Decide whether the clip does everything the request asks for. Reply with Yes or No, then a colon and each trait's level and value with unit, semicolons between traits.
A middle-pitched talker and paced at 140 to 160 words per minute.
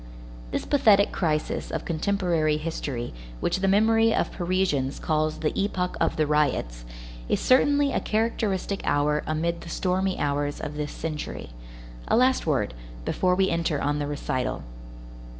Yes: medium, 165 Hz; average, 150 wpm